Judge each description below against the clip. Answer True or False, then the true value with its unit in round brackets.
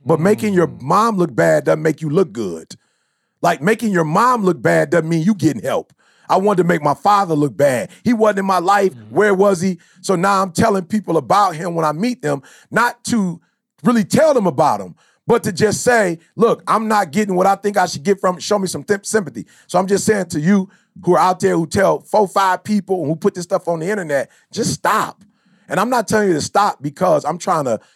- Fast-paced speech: True (245 wpm)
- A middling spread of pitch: True (3.4 semitones)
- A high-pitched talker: True (195 Hz)